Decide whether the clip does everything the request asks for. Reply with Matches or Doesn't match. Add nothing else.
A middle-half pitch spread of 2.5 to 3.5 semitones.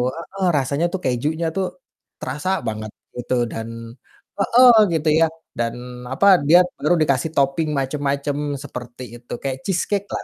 Doesn't match